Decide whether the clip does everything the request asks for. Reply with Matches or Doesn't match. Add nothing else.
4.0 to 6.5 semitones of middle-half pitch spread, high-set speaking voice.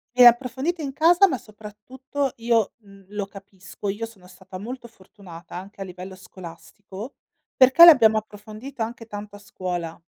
Matches